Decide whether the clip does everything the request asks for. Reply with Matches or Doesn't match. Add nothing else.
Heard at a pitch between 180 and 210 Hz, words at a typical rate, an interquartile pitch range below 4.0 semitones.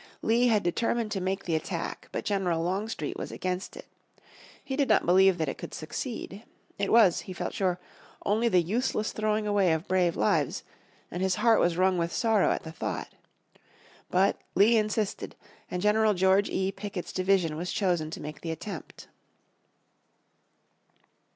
Matches